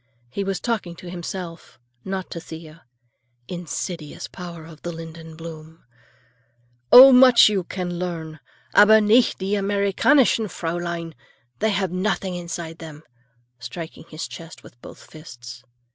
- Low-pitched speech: No, medium, 175 Hz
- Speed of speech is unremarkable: No, slow, 130 wpm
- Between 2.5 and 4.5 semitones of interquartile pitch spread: Yes, average, 3.3 semitones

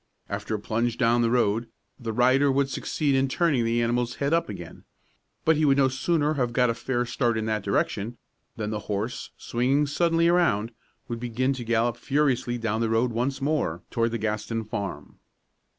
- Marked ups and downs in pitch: No, average, 3.3 semitones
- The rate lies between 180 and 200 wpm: Yes, average, 190 wpm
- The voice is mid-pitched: No, low, 120 Hz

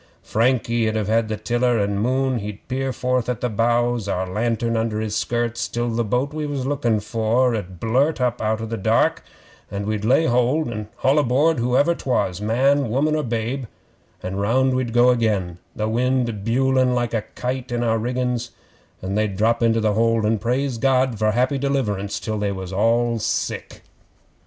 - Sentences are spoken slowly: No, average, 185 wpm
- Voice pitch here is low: Yes, low, 115 Hz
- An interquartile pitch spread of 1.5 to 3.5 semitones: Yes, average, 2.8 semitones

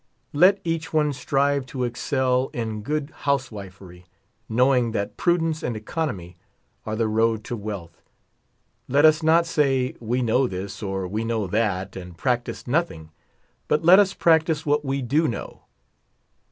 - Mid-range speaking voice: No, low, 125 Hz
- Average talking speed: Yes, average, 155 wpm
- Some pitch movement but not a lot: No, wide, 5.8 semitones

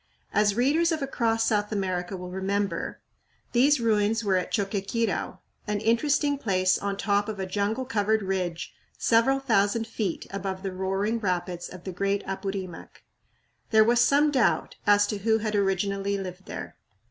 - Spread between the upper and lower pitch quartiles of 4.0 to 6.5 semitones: No, average, 2.9 semitones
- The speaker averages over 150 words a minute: Yes, average, 160 wpm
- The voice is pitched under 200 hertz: No, high, 205 Hz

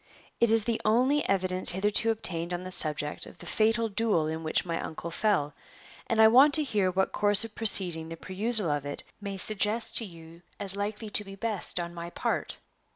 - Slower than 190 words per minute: No, fast, 205 wpm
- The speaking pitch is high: Yes, high, 200 Hz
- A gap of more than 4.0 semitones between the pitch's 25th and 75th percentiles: Yes, average, 4.5 semitones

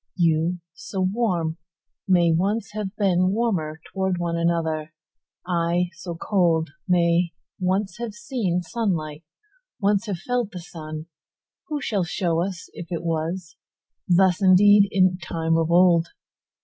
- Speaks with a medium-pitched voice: Yes, medium, 180 Hz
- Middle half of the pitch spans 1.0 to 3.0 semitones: Yes, average, 2.7 semitones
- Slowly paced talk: Yes, slow, 115 wpm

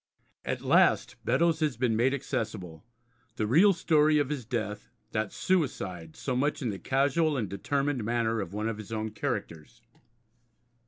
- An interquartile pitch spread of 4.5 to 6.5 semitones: Yes, average, 5.3 semitones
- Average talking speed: Yes, average, 160 wpm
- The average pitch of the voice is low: Yes, low, 120 Hz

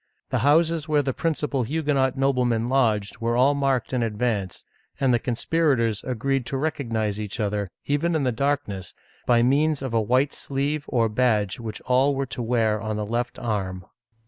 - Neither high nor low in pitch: No, low, 125 Hz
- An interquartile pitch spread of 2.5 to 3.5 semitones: No, average, 3.9 semitones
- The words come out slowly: No, average, 175 wpm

